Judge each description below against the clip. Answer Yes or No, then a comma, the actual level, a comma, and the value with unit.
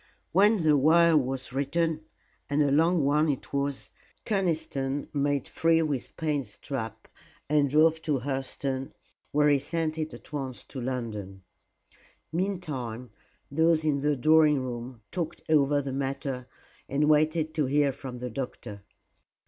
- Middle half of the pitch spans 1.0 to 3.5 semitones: Yes, average, 3.0 semitones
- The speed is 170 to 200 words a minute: No, average, 140 wpm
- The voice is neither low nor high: Yes, medium, 145 Hz